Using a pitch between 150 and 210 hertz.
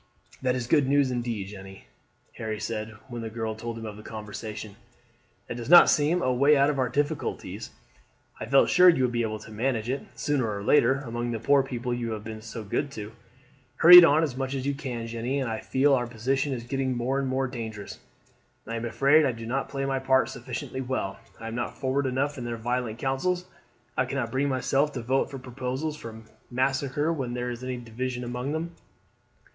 No: low, 125 Hz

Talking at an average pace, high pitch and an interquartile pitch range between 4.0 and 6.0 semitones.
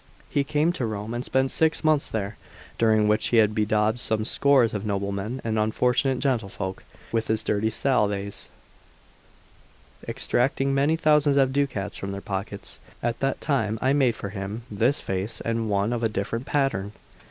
No: average, 165 wpm; low, 115 Hz; average, 4.5 semitones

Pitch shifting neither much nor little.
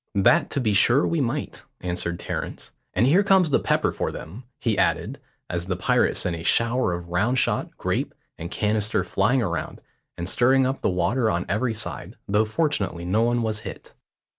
No: wide, 6.4 semitones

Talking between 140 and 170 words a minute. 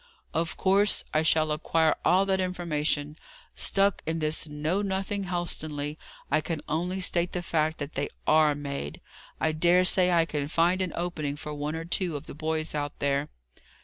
No: average, 180 wpm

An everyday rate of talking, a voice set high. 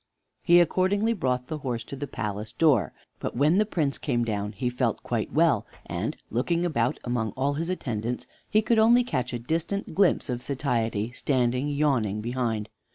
No: average, 175 wpm; low, 130 Hz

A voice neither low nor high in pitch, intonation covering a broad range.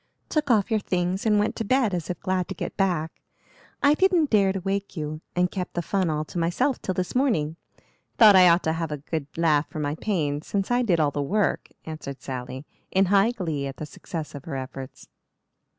No: medium, 180 Hz; average, 4.7 semitones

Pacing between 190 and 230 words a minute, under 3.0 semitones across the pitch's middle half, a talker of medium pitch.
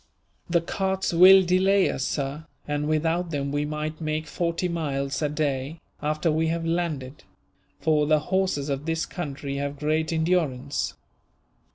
No: average, 150 wpm; narrow, 2.6 semitones; medium, 155 Hz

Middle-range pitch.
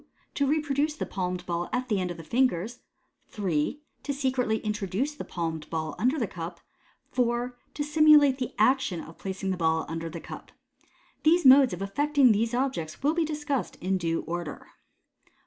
No: high, 230 Hz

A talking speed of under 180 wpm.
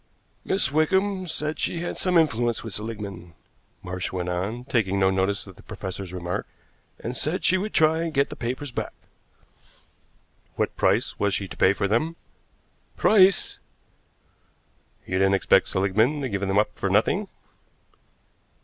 Yes: average, 155 wpm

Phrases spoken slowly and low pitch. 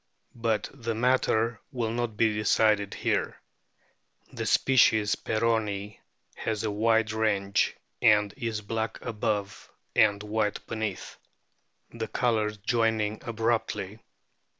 Yes: slow, 105 wpm; low, 110 Hz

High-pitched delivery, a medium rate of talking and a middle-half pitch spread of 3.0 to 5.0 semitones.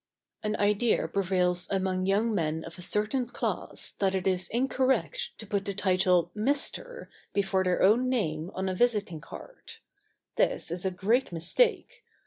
Yes: high, 195 Hz; average, 155 wpm; average, 4.2 semitones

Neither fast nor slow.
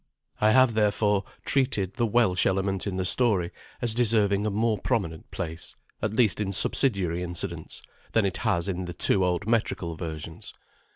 Yes: average, 165 wpm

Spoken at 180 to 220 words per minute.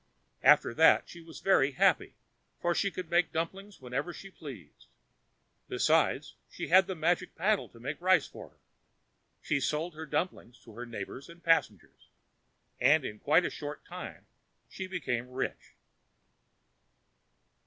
No: average, 145 wpm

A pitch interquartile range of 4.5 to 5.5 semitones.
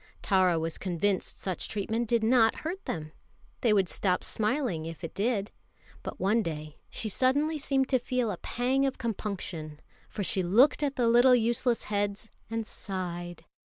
Yes: average, 5.2 semitones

